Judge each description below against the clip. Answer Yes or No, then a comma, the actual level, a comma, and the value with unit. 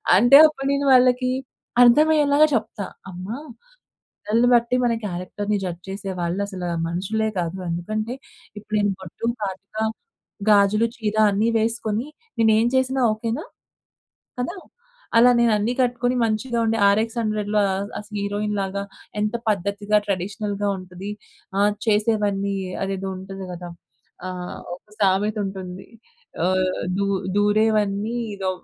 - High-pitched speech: Yes, high, 210 Hz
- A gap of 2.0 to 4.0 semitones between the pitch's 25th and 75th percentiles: Yes, average, 2.9 semitones